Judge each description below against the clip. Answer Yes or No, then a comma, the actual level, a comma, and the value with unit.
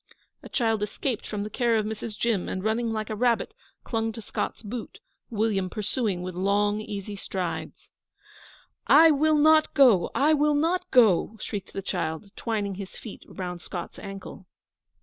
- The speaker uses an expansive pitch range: No, average, 3.4 semitones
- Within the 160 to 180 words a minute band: Yes, average, 165 wpm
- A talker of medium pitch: No, high, 215 Hz